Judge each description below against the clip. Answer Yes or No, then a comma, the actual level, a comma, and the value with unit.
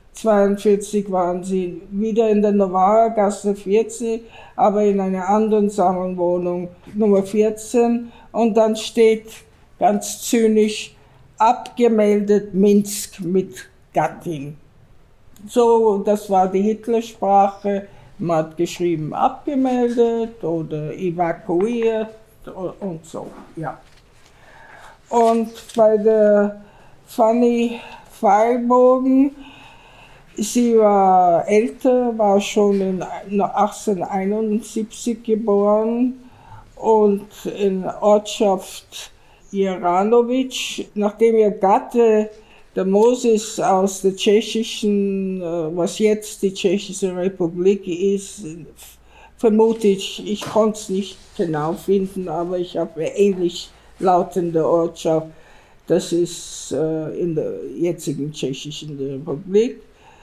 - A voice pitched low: No, high, 205 Hz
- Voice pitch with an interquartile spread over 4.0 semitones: No, average, 3.2 semitones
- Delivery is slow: Yes, slow, 90 wpm